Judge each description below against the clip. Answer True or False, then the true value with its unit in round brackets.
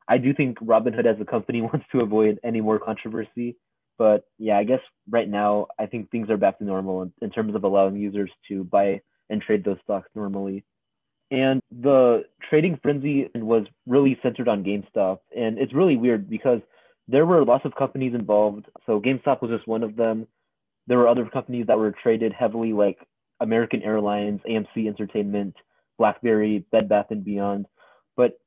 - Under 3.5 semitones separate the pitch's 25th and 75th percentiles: True (2.9 semitones)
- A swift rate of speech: False (180 wpm)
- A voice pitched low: True (110 Hz)